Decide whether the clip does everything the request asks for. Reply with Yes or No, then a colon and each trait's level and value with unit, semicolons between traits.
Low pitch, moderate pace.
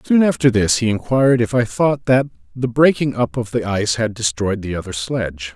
No: low, 115 Hz; fast, 215 wpm